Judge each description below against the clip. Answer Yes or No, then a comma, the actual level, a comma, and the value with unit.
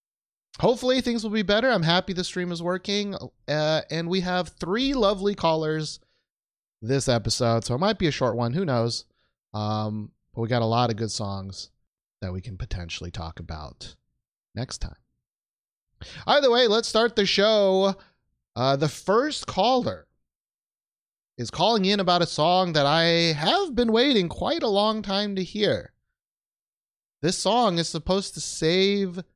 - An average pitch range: No, wide, 8.9 semitones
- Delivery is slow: No, average, 160 wpm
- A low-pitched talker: No, medium, 170 Hz